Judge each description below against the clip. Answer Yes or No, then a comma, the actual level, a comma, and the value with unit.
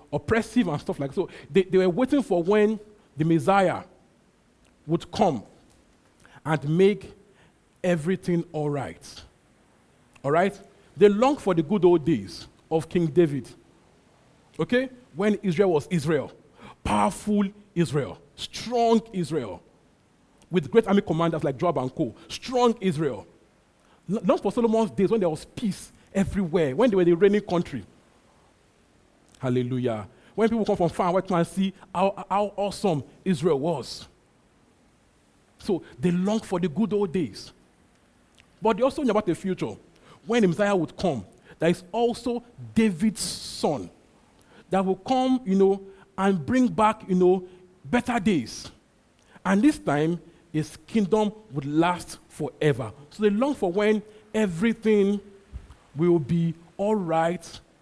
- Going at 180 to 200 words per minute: No, average, 140 wpm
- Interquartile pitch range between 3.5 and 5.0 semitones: Yes, average, 4.4 semitones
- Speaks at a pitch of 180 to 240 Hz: Yes, medium, 185 Hz